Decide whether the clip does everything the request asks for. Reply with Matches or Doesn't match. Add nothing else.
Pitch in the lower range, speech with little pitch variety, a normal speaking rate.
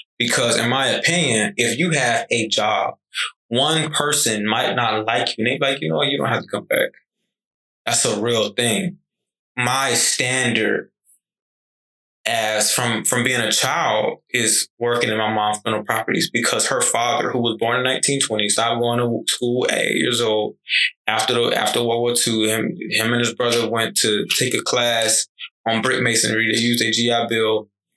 Matches